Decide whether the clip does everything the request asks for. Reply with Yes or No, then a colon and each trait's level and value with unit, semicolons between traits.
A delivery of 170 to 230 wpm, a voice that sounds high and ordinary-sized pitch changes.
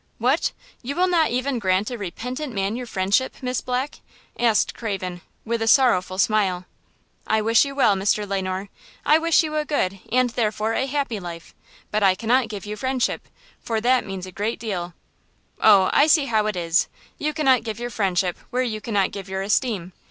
Yes: average, 195 wpm; high, 220 Hz; average, 4.7 semitones